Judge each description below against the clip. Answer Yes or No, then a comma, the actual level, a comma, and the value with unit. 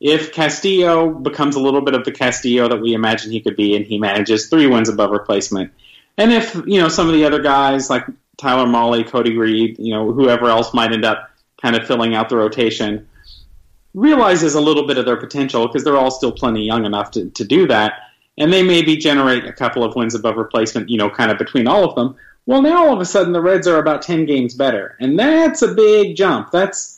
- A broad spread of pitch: Yes, wide, 6.1 semitones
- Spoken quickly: Yes, fast, 230 wpm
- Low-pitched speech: Yes, low, 130 Hz